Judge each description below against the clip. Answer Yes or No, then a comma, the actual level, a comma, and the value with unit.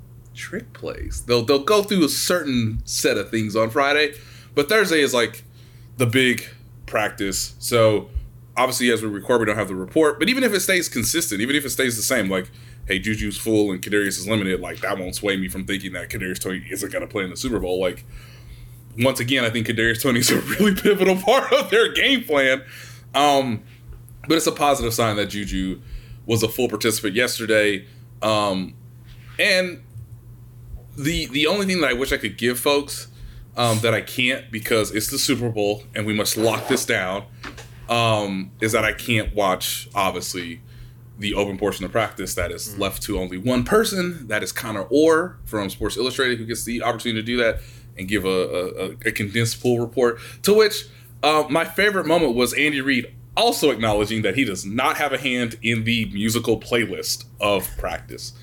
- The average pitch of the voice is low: Yes, low, 120 Hz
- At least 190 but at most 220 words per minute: Yes, average, 195 wpm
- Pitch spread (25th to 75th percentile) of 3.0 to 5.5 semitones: Yes, average, 3.3 semitones